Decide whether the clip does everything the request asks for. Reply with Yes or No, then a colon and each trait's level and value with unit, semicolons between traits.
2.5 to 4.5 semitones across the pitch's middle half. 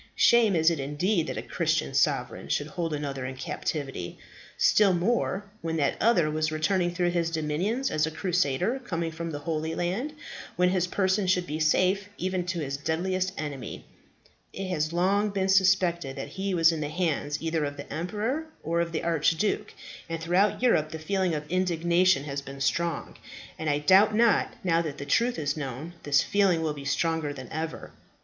Yes: average, 3.6 semitones